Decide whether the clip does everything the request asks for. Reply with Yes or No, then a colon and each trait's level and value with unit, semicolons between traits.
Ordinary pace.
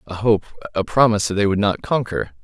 Yes: average, 195 wpm